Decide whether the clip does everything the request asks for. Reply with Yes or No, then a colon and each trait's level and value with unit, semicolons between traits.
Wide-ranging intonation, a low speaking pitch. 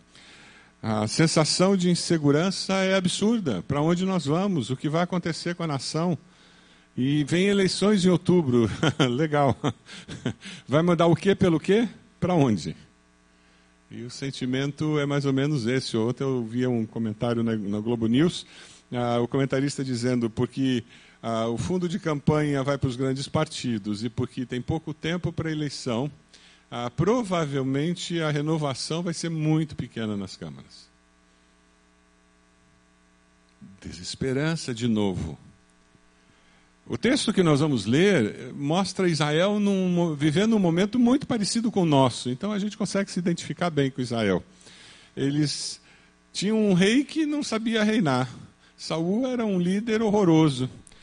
No: wide, 7.5 semitones; medium, 145 Hz